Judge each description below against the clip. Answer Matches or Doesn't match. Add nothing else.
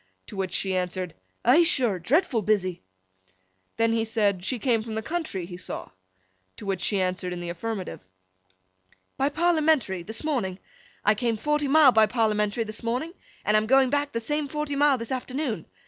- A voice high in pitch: Matches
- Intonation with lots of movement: Matches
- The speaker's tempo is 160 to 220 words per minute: Matches